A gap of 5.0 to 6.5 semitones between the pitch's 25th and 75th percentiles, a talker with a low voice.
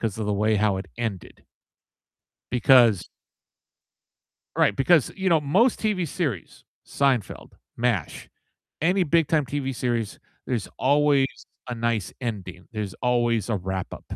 Yes: average, 5.3 semitones; low, 120 Hz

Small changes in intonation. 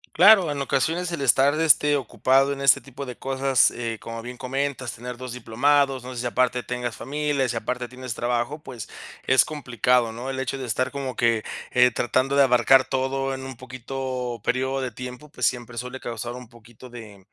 Yes: narrow, 2.0 semitones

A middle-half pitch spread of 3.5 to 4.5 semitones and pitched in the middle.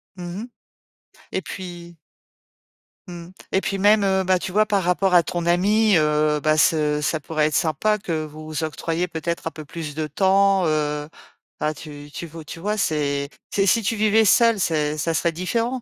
Yes: average, 4.1 semitones; medium, 170 Hz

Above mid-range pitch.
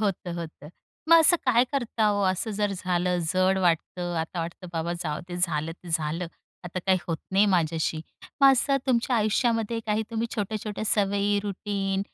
Yes: high, 195 Hz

